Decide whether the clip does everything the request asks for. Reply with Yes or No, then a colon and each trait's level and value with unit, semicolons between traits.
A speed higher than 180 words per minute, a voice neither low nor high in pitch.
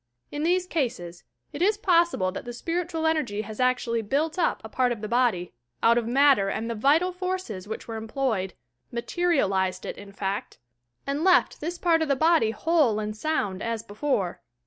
No: average, 195 wpm; high, 245 Hz